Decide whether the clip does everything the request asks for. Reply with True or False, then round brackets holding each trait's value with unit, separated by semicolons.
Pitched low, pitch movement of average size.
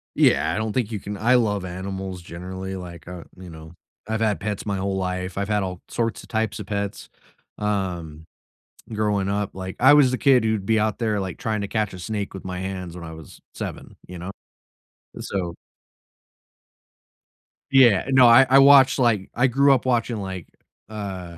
True (100 Hz; 3.3 semitones)